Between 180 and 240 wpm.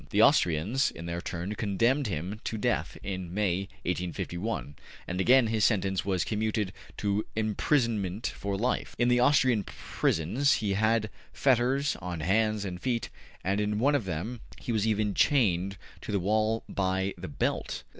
No: average, 160 wpm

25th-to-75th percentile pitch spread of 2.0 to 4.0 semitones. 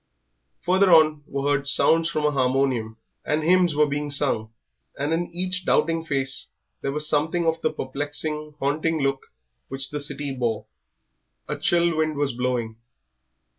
Yes: average, 3.0 semitones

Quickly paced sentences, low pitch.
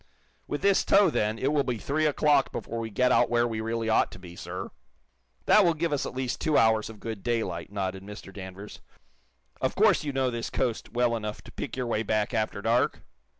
Yes: fast, 220 wpm; low, 115 Hz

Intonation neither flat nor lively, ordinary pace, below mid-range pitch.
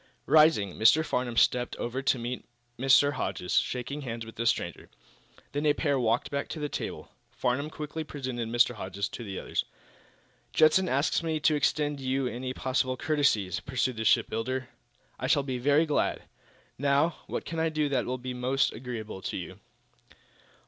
Yes: average, 3.5 semitones; average, 175 wpm; low, 130 Hz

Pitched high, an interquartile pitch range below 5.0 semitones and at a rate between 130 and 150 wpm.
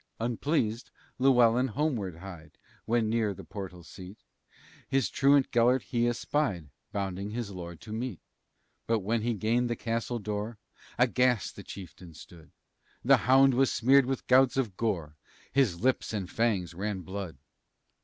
No: low, 115 Hz; average, 4.5 semitones; average, 145 wpm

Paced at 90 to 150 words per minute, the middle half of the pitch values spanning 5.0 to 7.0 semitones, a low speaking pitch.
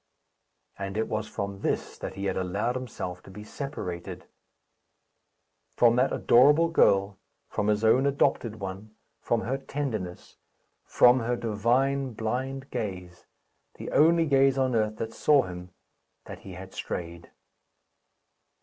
Yes: slow, 135 wpm; average, 5.3 semitones; low, 110 Hz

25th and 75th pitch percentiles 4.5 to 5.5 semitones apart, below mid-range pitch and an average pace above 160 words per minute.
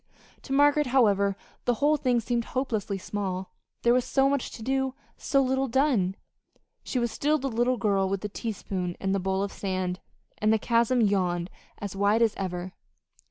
No: average, 5.0 semitones; high, 220 Hz; average, 180 wpm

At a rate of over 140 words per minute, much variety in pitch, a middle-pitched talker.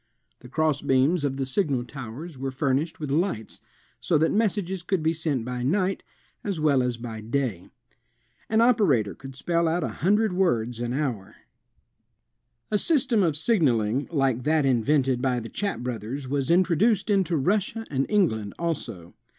Yes: average, 165 wpm; wide, 6.2 semitones; medium, 145 Hz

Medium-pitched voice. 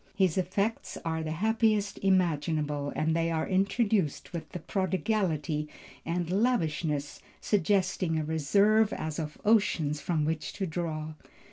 Yes: medium, 170 Hz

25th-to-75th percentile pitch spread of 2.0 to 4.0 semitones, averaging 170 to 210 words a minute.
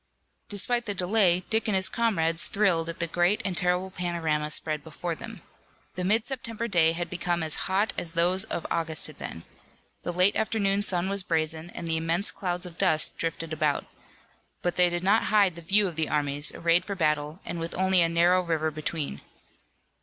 Yes: average, 2.9 semitones; average, 190 wpm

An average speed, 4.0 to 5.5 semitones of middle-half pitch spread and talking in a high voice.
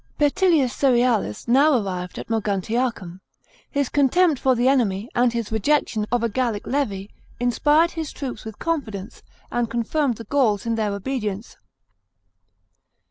Yes: average, 150 wpm; average, 4.6 semitones; high, 240 Hz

